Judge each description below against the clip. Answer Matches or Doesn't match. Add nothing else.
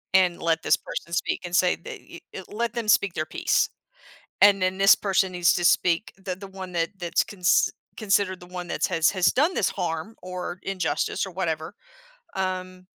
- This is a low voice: Doesn't match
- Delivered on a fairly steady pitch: Matches